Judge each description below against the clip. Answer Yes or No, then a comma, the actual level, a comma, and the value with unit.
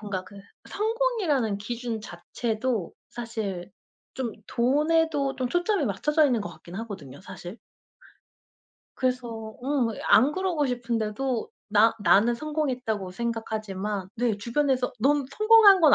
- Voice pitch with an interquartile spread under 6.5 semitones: Yes, wide, 5.4 semitones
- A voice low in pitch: No, high, 240 Hz